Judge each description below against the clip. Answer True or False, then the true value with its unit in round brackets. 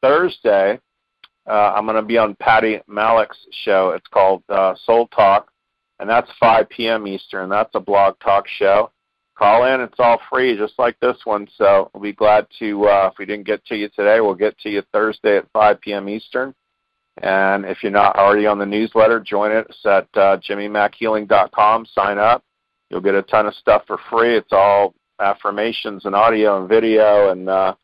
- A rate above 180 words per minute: True (190 wpm)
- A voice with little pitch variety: True (2.1 semitones)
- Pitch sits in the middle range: False (105 Hz)